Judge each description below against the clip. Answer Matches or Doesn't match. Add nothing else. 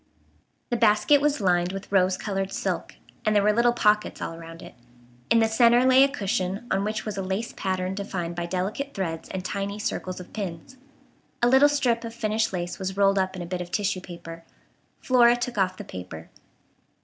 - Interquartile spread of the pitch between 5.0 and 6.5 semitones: Doesn't match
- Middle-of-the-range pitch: Doesn't match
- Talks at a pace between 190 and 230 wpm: Matches